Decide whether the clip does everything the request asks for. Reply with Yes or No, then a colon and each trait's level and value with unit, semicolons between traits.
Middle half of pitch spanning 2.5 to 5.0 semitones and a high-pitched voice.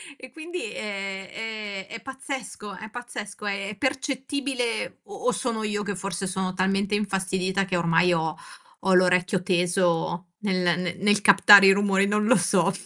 Yes: average, 2.9 semitones; high, 200 Hz